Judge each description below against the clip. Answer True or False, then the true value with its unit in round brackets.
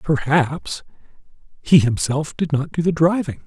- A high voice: False (150 Hz)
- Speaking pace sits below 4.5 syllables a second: True (4.3 syllables/s)